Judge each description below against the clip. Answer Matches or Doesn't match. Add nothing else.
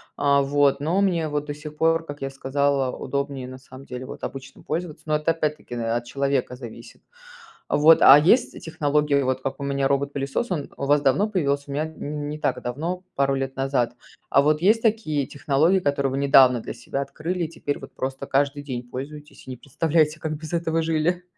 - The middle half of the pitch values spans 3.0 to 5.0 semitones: Doesn't match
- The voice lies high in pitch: Doesn't match